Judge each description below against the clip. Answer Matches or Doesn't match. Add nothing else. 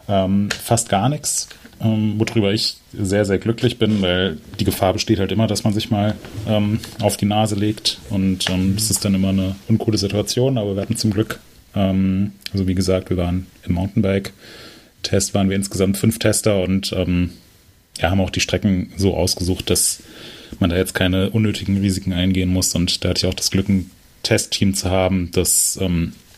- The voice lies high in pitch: Doesn't match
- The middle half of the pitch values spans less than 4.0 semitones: Matches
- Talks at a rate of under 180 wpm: Doesn't match